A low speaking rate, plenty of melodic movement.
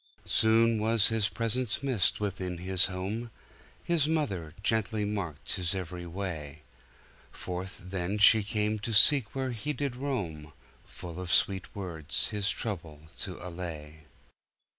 No: slow, 130 wpm; average, 4.3 semitones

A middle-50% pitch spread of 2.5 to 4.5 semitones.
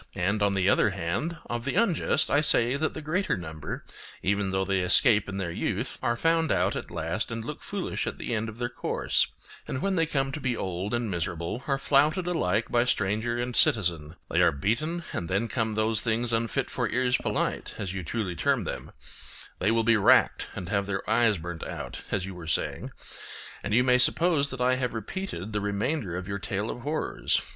No: average, 5.3 semitones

